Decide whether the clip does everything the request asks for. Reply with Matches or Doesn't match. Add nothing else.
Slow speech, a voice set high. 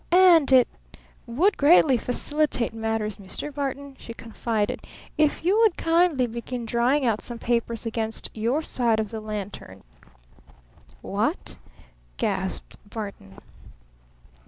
Matches